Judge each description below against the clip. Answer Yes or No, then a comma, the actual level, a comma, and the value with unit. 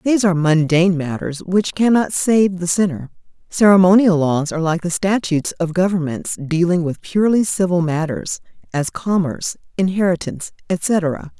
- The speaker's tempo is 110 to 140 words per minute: Yes, slow, 135 wpm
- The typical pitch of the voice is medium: Yes, medium, 175 Hz